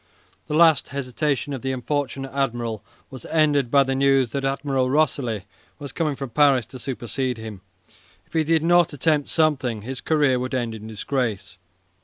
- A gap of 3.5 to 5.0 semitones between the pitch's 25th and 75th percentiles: No, average, 3.0 semitones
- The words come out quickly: No, average, 170 wpm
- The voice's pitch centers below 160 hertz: Yes, low, 135 Hz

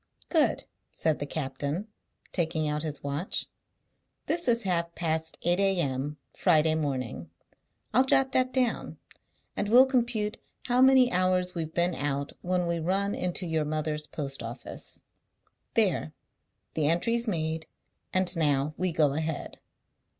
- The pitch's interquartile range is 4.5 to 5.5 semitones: Yes, average, 4.8 semitones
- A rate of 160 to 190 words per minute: No, slow, 135 wpm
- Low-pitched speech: No, medium, 170 Hz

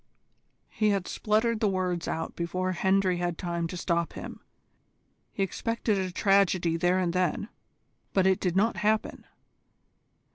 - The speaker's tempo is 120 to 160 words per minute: Yes, average, 145 wpm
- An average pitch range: No, narrow, 2.3 semitones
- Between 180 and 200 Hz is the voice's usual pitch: Yes, medium, 185 Hz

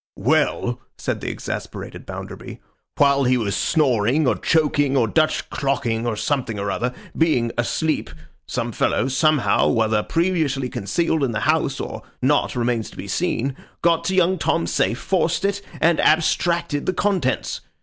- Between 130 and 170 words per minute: Yes, average, 150 wpm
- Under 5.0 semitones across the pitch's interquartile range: No, average, 5.3 semitones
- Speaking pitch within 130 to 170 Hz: Yes, medium, 140 Hz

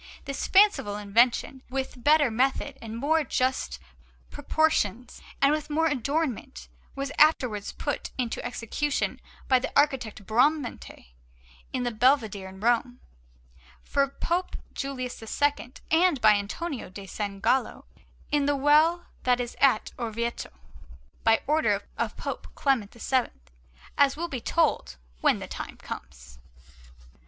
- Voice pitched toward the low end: No, very high, 260 Hz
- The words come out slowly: Yes, slow, 130 wpm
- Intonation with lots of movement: No, average, 4.6 semitones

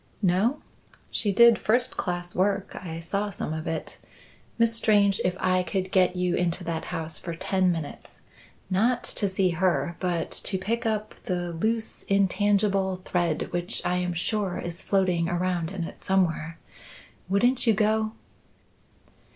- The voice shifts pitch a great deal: No, average, 2.8 semitones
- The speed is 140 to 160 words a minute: Yes, average, 150 wpm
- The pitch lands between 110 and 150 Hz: No, medium, 185 Hz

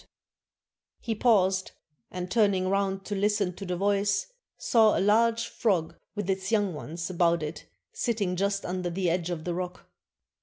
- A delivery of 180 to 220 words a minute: No, average, 165 wpm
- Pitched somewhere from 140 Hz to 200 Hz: Yes, high, 190 Hz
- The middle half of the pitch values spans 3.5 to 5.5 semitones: No, narrow, 2.4 semitones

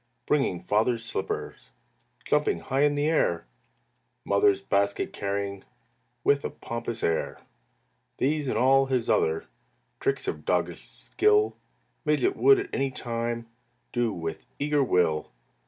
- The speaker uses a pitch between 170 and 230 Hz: No, low, 120 Hz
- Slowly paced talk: Yes, slow, 120 wpm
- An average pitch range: No, wide, 6.7 semitones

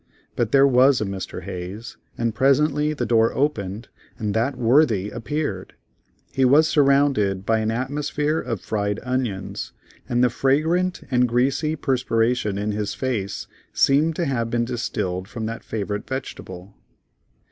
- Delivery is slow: No, average, 145 wpm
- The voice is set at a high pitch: No, low, 120 Hz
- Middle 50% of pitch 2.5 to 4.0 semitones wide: No, average, 4.7 semitones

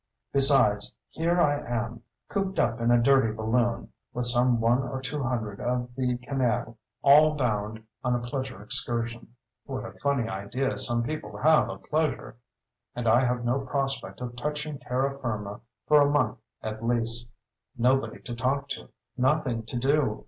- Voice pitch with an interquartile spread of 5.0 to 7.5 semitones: No, average, 2.7 semitones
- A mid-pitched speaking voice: No, low, 125 Hz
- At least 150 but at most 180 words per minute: Yes, average, 165 wpm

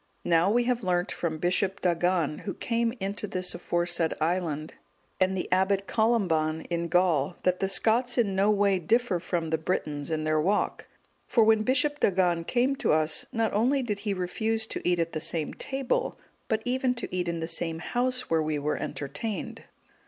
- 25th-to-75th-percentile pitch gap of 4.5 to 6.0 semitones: Yes, average, 5.1 semitones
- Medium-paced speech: Yes, average, 185 wpm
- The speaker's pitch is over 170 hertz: Yes, medium, 185 Hz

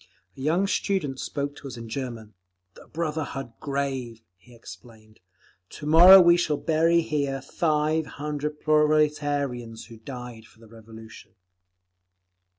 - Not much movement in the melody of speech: No, average, 4.6 semitones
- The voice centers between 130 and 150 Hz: Yes, medium, 140 Hz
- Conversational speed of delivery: No, slow, 130 wpm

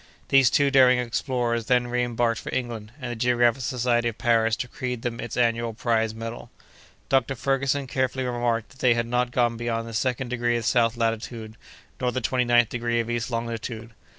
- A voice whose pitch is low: Yes, low, 120 Hz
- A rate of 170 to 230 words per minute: Yes, average, 180 wpm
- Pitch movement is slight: Yes, narrow, 1.4 semitones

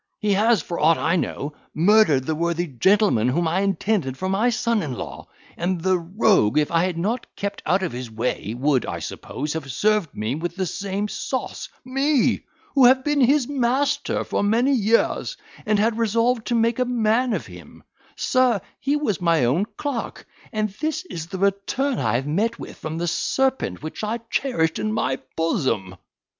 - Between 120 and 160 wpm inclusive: No, average, 185 wpm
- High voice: Yes, high, 200 Hz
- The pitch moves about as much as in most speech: No, wide, 6.5 semitones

